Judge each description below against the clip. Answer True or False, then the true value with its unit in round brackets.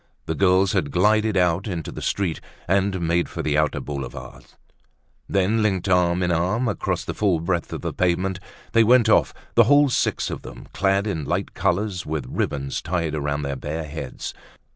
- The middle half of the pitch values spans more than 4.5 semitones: False (3.5 semitones)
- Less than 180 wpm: False (185 wpm)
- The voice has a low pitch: True (90 Hz)